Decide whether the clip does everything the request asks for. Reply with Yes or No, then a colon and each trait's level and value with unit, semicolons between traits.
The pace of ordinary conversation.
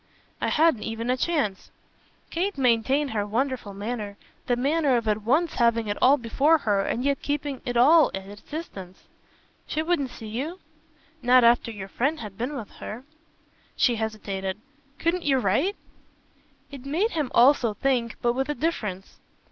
Yes: average, 165 wpm